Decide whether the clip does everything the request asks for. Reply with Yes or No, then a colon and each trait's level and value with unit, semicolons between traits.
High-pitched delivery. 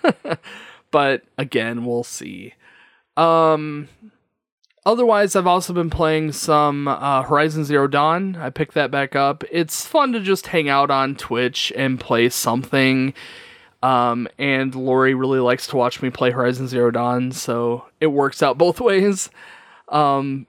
No: medium, 140 Hz